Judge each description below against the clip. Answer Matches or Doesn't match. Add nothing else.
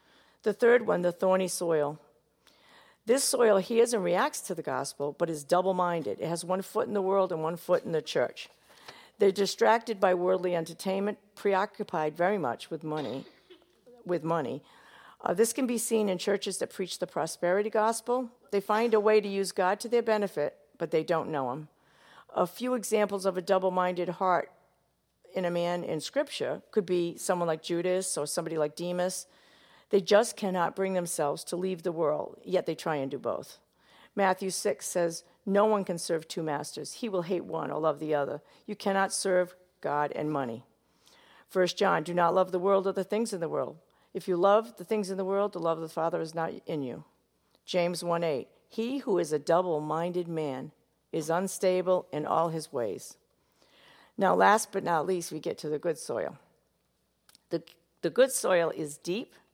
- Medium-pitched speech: Matches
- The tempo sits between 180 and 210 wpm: Matches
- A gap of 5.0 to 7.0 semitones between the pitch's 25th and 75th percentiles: Doesn't match